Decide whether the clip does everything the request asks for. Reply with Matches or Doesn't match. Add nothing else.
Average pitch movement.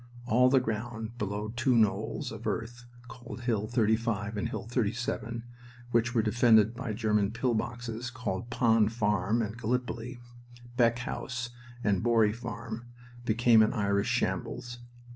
Doesn't match